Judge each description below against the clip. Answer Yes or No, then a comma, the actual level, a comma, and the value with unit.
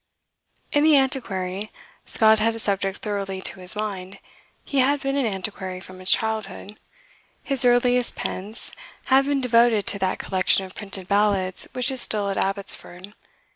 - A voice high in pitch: Yes, high, 210 Hz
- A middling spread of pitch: Yes, average, 4.2 semitones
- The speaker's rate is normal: Yes, average, 160 wpm